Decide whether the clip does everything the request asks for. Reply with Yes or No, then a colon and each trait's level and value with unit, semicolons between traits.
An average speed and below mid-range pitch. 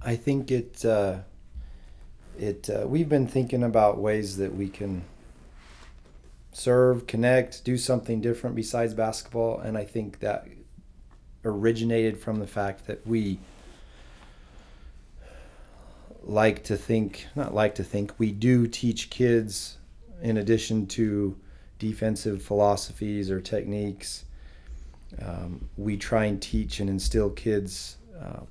No: slow, 120 wpm; low, 105 Hz